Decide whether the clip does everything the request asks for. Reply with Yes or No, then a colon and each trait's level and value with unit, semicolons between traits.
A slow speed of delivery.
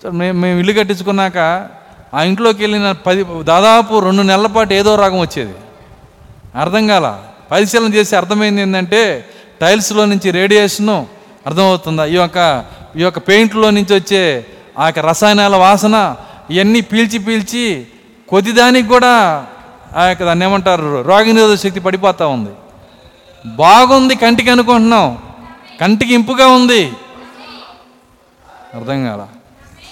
No: average, 115 wpm